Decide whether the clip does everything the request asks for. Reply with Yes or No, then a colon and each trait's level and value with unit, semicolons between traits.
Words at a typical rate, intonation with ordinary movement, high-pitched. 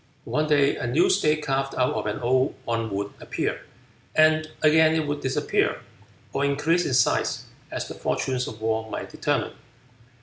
No: average, 170 wpm; average, 4.6 semitones; low, 135 Hz